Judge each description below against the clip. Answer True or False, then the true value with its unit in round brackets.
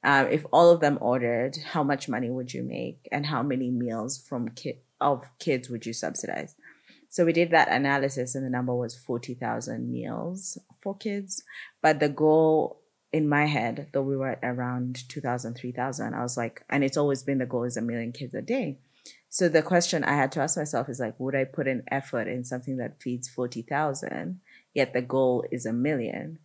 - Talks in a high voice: False (130 Hz)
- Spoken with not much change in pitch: False (3.3 semitones)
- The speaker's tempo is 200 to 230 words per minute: True (205 wpm)